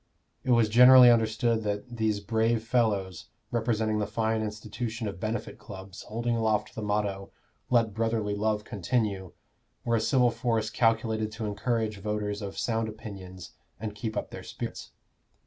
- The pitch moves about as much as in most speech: No, narrow, 1.8 semitones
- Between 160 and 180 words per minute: No, average, 150 wpm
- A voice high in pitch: No, low, 110 Hz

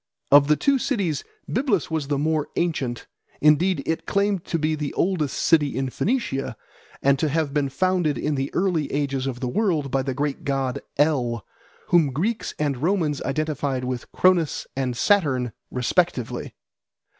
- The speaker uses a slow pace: No, average, 160 wpm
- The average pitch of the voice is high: No, medium, 150 Hz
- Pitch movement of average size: Yes, average, 4.2 semitones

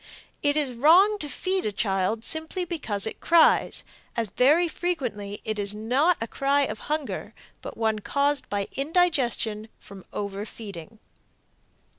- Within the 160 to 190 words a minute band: No, average, 140 wpm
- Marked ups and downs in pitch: Yes, wide, 7.0 semitones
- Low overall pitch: No, very high, 250 Hz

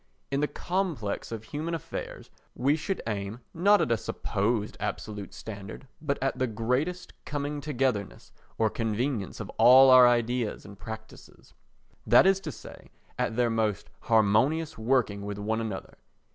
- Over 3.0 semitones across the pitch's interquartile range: Yes, average, 4.9 semitones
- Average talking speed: Yes, average, 155 wpm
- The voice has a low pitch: Yes, low, 120 Hz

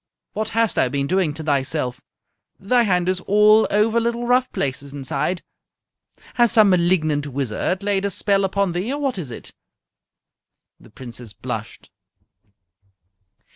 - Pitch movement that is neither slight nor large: No, wide, 7.0 semitones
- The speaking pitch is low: No, medium, 185 Hz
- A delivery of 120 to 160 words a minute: Yes, average, 140 wpm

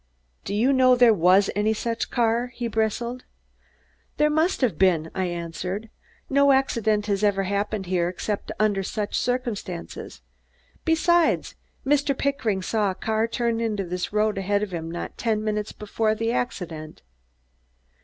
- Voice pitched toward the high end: Yes, high, 215 Hz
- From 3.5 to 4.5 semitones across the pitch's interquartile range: Yes, average, 3.9 semitones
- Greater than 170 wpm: No, average, 150 wpm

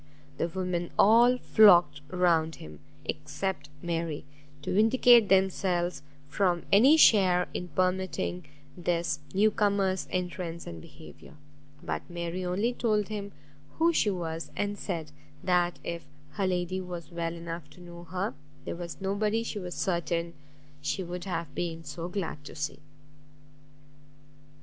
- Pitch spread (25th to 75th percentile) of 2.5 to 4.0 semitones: Yes, average, 2.8 semitones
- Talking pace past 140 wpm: No, slow, 135 wpm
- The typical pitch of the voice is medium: Yes, medium, 180 Hz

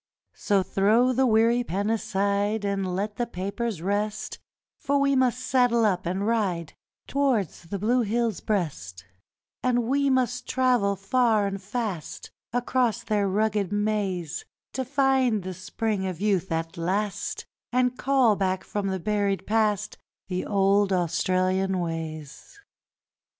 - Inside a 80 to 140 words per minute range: Yes, slow, 135 wpm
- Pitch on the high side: Yes, high, 205 Hz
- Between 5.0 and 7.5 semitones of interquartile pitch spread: No, average, 4.1 semitones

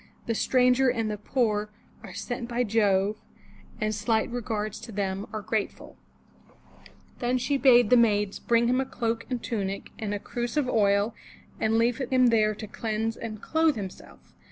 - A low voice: No, high, 225 Hz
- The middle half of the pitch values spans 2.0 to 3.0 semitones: Yes, average, 2.7 semitones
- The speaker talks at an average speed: Yes, average, 170 wpm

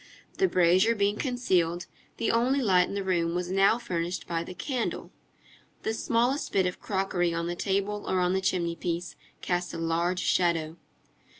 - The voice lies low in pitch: No, medium, 185 Hz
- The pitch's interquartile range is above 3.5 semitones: No, average, 3.2 semitones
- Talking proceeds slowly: No, average, 175 wpm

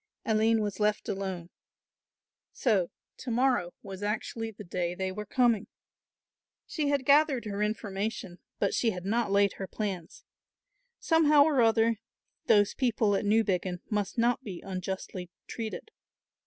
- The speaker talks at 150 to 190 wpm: No, average, 140 wpm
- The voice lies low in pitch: No, high, 210 Hz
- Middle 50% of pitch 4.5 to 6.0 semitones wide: No, average, 3.4 semitones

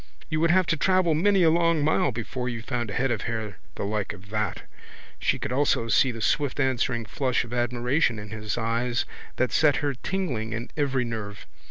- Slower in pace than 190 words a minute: No, fast, 205 wpm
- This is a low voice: Yes, low, 125 Hz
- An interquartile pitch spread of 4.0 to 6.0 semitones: Yes, average, 4.5 semitones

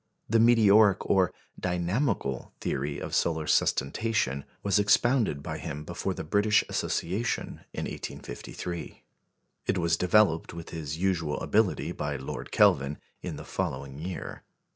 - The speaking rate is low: Yes, slow, 130 wpm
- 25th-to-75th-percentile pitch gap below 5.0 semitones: No, wide, 5.5 semitones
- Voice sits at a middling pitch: No, very low, 85 Hz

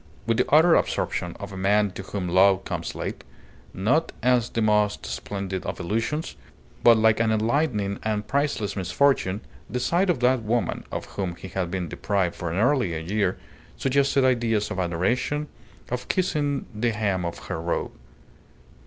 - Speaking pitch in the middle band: No, low, 110 Hz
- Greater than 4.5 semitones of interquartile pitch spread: Yes, average, 4.9 semitones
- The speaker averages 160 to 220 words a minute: Yes, average, 165 wpm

